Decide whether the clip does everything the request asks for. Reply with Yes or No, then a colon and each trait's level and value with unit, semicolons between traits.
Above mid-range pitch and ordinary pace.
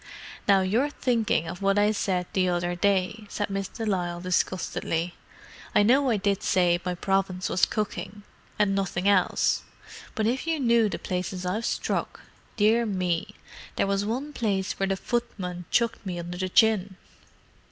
Yes: high, 195 Hz; average, 165 wpm